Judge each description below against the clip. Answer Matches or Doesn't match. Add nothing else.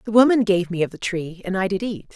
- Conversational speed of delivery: Doesn't match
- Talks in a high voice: Matches